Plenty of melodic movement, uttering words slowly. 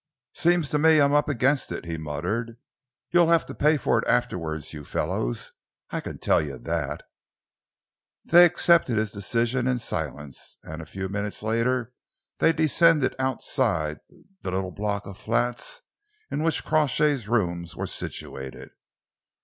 No: wide, 8.8 semitones; average, 150 wpm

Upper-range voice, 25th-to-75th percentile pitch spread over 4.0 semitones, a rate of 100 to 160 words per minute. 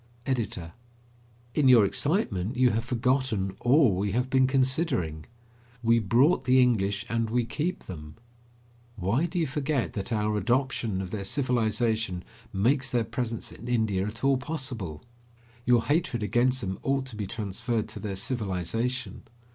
No: low, 115 Hz; average, 4.4 semitones; average, 150 wpm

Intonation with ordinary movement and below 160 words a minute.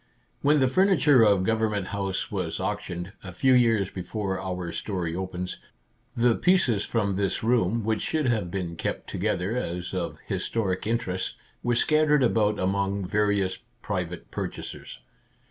Yes: average, 4.0 semitones; average, 150 wpm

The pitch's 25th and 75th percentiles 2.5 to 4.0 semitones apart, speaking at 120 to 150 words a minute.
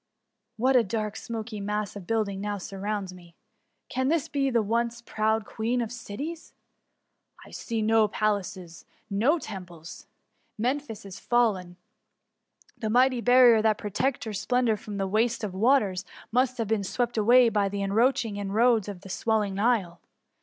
No: average, 3.2 semitones; average, 160 wpm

